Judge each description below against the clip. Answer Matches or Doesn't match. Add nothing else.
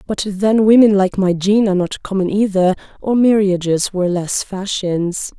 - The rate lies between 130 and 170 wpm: Matches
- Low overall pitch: Doesn't match